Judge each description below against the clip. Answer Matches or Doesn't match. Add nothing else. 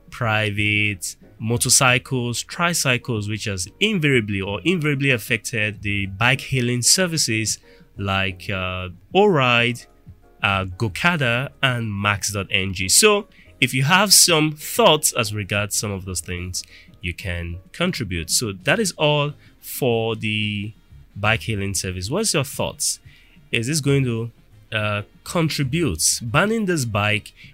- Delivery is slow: Matches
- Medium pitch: Doesn't match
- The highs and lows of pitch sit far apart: Matches